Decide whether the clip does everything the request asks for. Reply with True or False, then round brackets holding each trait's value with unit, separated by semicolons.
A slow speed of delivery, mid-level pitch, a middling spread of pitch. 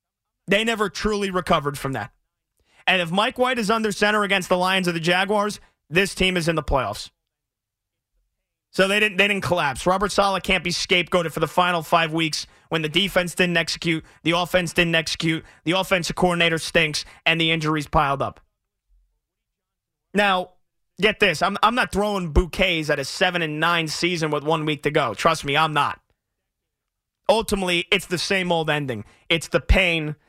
False (180 wpm; 175 Hz; 3.1 semitones)